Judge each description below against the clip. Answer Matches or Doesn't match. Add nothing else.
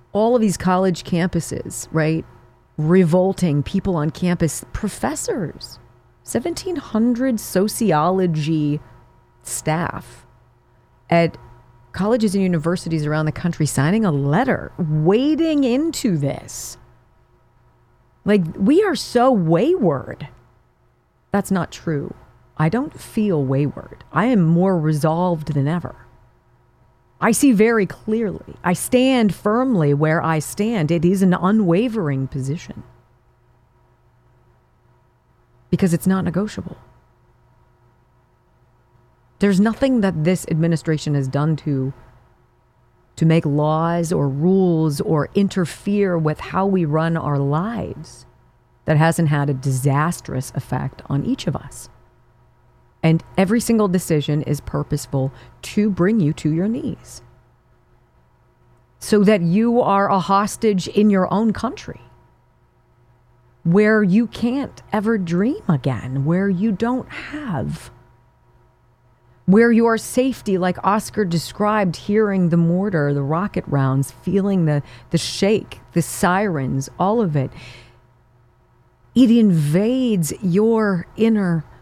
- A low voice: Doesn't match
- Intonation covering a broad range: Matches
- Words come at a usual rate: Doesn't match